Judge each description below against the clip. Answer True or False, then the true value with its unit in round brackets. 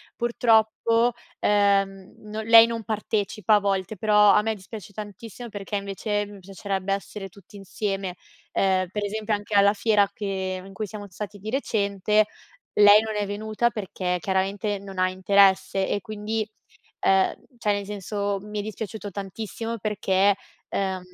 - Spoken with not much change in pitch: True (1.7 semitones)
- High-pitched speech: True (205 Hz)